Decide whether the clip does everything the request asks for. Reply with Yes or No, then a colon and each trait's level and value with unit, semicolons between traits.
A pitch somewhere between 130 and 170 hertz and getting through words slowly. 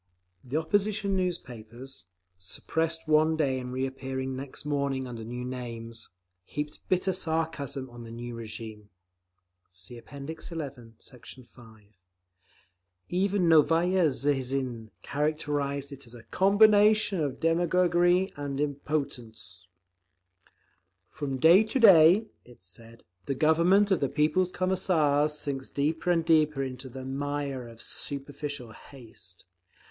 Yes: medium, 140 Hz; slow, 120 wpm